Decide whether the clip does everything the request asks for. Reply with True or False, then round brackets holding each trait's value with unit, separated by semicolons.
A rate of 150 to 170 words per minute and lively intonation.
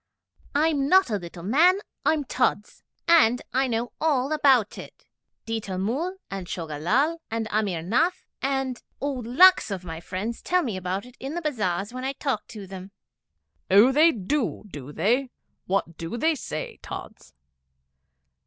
True (160 wpm; 6.7 semitones)